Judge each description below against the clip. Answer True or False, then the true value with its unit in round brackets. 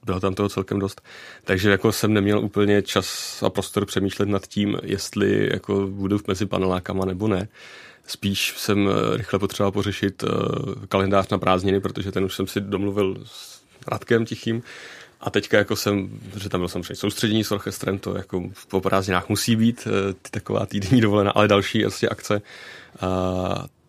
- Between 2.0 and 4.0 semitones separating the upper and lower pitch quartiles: False (1.4 semitones)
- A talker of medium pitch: False (100 Hz)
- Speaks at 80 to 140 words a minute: False (170 wpm)